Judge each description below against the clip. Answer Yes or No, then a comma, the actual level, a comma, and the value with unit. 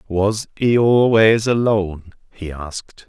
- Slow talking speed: Yes, slow, 115 wpm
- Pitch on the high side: No, low, 105 Hz